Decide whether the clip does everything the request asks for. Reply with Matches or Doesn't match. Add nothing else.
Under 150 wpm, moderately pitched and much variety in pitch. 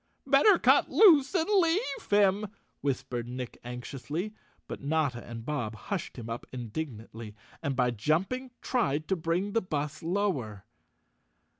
Matches